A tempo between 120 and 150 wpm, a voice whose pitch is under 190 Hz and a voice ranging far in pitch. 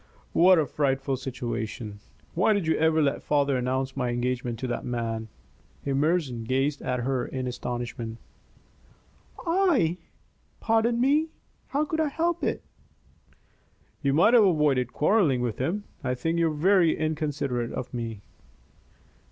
Yes: average, 140 wpm; medium, 140 Hz; wide, 6.0 semitones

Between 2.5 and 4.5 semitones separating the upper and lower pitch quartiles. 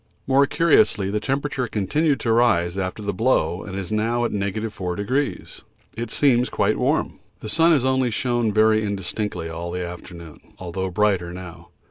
No: average, 5.0 semitones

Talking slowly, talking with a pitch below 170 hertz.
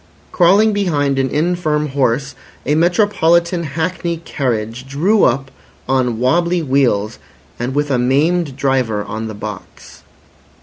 Yes: slow, 125 wpm; medium, 140 Hz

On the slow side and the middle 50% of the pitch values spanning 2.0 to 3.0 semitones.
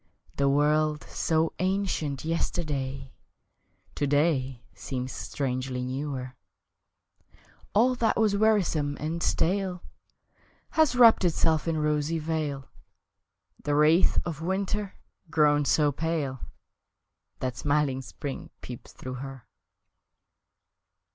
No: slow, 100 wpm; average, 3.7 semitones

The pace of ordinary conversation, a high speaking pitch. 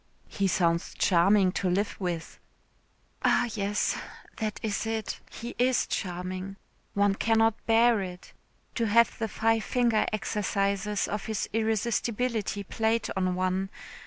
No: slow, 130 wpm; high, 210 Hz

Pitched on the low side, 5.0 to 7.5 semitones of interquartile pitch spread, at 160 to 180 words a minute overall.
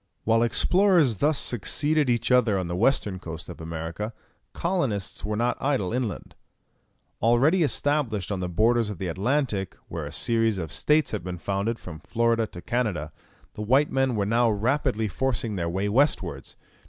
Yes: low, 115 Hz; average, 5.3 semitones; average, 165 wpm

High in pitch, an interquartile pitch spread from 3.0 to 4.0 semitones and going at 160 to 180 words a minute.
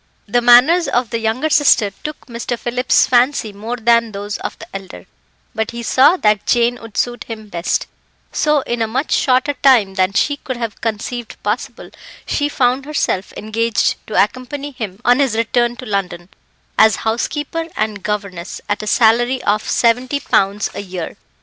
Yes: high, 235 Hz; average, 3.3 semitones; average, 170 wpm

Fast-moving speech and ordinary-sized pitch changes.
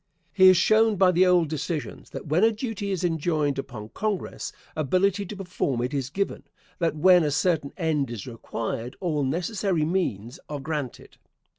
No: average, 170 wpm; average, 4.9 semitones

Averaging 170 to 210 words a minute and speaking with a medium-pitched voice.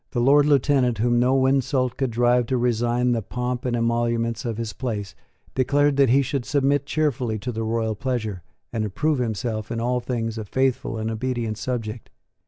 No: average, 185 wpm; low, 120 Hz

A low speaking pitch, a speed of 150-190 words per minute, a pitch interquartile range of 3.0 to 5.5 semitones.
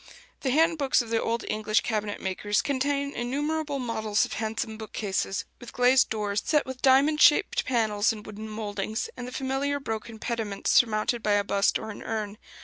No: high, 225 Hz; average, 180 wpm; average, 3.8 semitones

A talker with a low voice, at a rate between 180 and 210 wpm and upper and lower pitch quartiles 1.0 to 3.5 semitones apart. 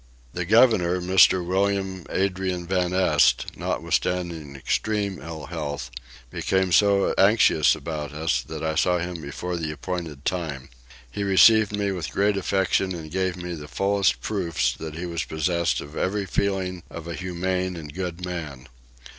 No: very low, 90 Hz; average, 155 wpm; average, 3.1 semitones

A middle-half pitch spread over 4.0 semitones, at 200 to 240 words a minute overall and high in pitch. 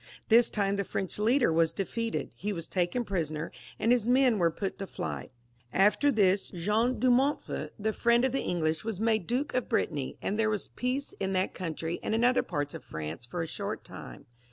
Yes: wide, 5.5 semitones; fast, 205 wpm; high, 205 Hz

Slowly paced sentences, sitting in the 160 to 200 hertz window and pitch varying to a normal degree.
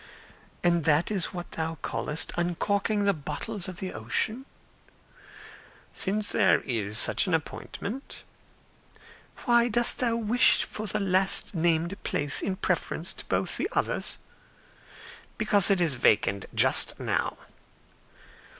Yes: slow, 125 wpm; medium, 185 Hz; average, 4.7 semitones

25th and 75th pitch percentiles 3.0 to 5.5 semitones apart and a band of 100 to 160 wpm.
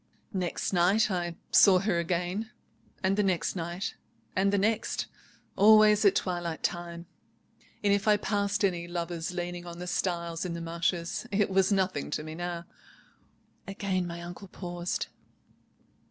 No: narrow, 2.5 semitones; average, 150 wpm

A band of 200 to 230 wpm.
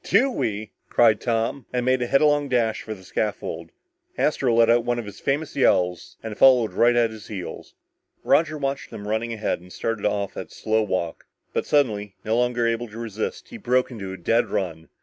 Yes: fast, 205 wpm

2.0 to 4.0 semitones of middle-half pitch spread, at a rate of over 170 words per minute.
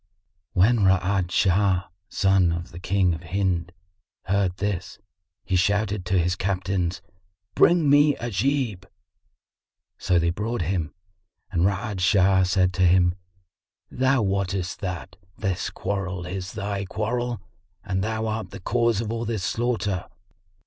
No: average, 2.9 semitones; slow, 135 wpm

